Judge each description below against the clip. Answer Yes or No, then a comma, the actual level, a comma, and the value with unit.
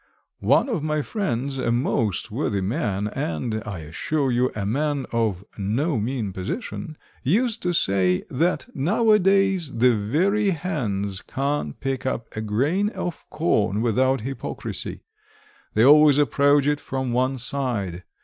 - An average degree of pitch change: No, wide, 6.2 semitones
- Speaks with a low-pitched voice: Yes, low, 130 Hz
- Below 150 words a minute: Yes, average, 140 wpm